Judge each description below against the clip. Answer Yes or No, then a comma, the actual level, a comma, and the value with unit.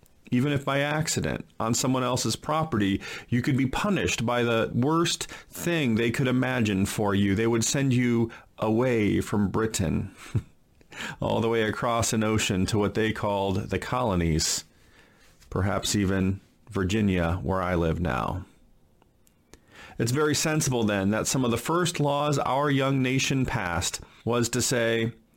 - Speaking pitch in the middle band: No, low, 115 Hz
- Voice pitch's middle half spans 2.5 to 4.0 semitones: No, average, 4.4 semitones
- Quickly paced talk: No, average, 150 wpm